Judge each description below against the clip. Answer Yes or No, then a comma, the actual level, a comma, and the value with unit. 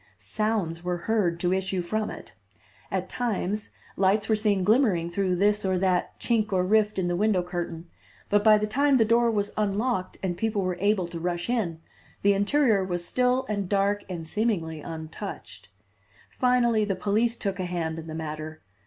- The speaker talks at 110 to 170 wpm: No, average, 180 wpm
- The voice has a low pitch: No, high, 195 Hz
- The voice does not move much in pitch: No, average, 3.6 semitones